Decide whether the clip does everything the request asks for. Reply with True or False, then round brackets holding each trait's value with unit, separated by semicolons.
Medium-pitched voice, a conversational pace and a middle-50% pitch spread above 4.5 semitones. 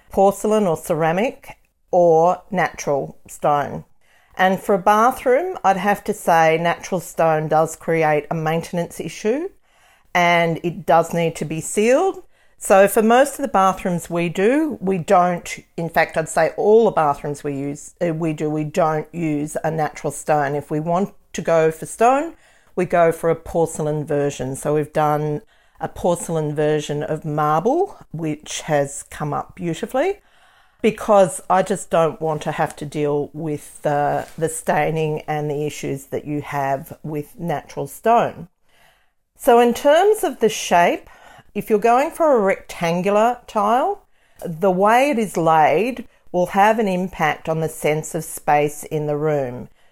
True (170 Hz; 160 wpm; 5.4 semitones)